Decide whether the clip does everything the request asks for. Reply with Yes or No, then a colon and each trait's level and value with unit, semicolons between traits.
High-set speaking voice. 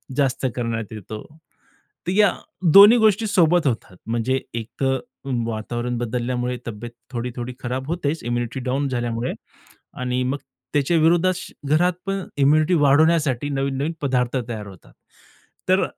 No: low, 130 Hz